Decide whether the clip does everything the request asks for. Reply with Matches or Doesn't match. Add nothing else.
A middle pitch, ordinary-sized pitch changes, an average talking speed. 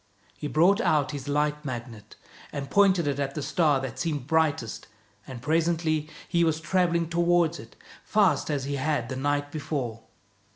Matches